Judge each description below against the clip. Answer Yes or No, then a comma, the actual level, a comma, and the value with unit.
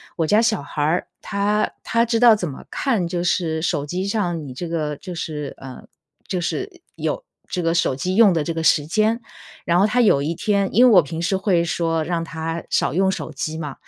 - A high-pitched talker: No, medium, 175 Hz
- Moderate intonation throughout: Yes, average, 4.1 semitones